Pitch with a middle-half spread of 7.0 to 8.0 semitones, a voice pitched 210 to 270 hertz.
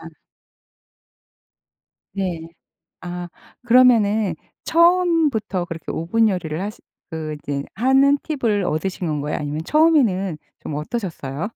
No: wide, 7.4 semitones; high, 190 Hz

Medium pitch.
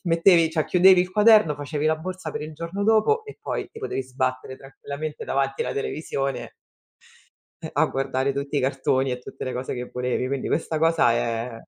Yes: medium, 145 Hz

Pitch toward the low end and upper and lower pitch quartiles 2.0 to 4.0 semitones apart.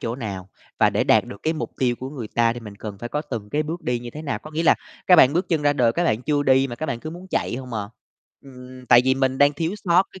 No: low, 130 Hz; average, 4.5 semitones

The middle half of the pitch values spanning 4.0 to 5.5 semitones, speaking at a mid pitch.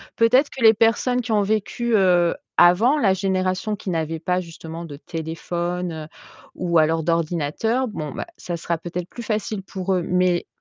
Yes: average, 4.3 semitones; medium, 180 Hz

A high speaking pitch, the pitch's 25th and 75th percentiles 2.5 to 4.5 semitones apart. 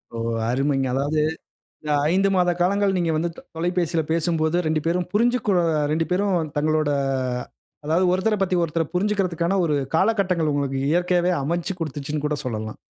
No: medium, 170 Hz; average, 3.3 semitones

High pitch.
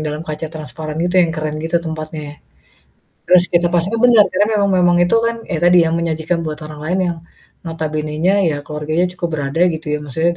No: medium, 160 Hz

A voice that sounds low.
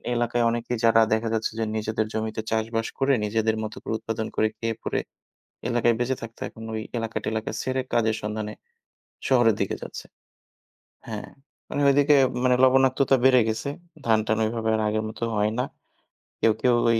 Yes: low, 115 Hz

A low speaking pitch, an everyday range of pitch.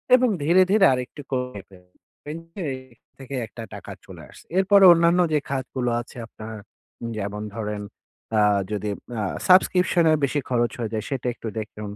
No: low, 125 Hz; wide, 7.6 semitones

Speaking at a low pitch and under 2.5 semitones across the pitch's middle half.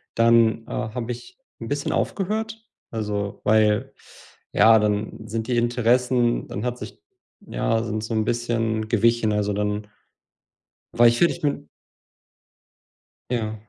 Yes: low, 115 Hz; narrow, 2.0 semitones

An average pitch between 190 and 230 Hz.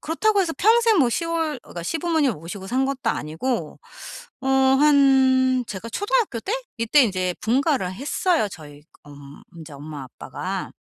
No: very high, 260 Hz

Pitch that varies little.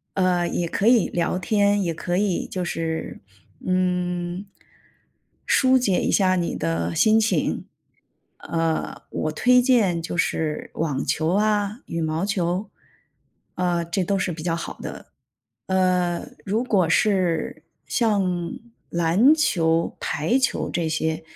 No: average, 3.4 semitones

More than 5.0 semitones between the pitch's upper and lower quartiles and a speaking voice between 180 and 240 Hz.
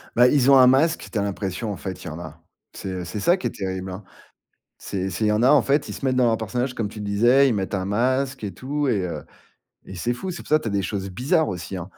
No: wide, 5.5 semitones; low, 110 Hz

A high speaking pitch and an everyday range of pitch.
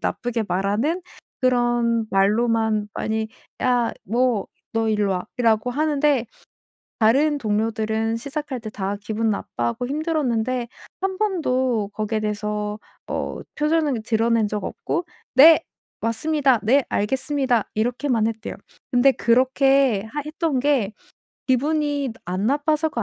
Yes: high, 240 Hz; average, 4.5 semitones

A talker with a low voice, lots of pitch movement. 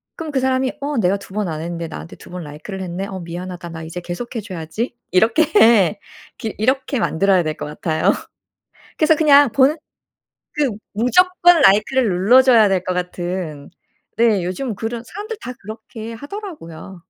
No: high, 210 Hz; wide, 6.7 semitones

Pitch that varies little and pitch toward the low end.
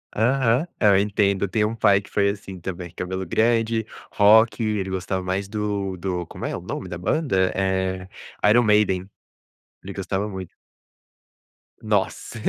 Yes: narrow, 2.3 semitones; low, 100 Hz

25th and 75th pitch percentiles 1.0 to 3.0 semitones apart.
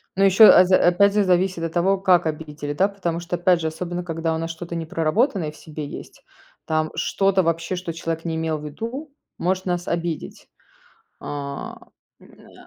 Yes: narrow, 2.6 semitones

